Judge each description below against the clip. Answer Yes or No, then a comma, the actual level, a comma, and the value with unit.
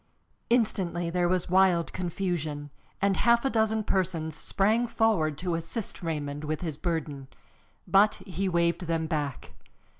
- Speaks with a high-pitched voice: No, medium, 175 Hz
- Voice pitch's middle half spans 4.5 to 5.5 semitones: No, average, 3.7 semitones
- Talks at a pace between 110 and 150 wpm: Yes, average, 140 wpm